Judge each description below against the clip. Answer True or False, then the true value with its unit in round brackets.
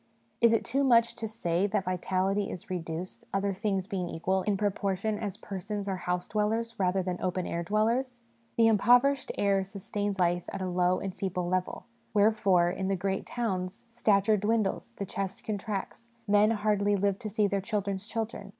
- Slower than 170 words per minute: False (180 wpm)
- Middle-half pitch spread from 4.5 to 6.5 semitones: False (2.5 semitones)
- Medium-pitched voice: False (200 Hz)